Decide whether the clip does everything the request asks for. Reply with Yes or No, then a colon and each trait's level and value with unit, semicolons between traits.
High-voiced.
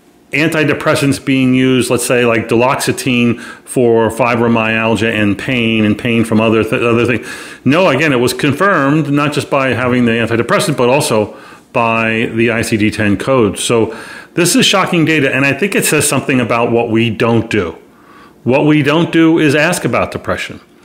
No: low, 125 Hz